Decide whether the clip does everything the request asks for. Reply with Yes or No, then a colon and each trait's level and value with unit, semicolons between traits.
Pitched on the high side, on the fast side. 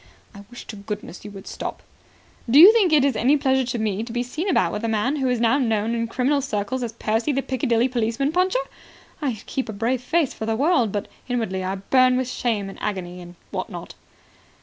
Yes: high, 240 Hz; fast, 225 wpm